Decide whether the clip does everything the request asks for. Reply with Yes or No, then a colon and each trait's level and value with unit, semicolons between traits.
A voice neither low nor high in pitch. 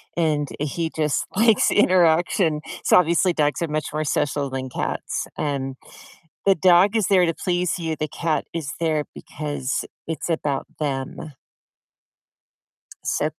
Yes: medium, 160 Hz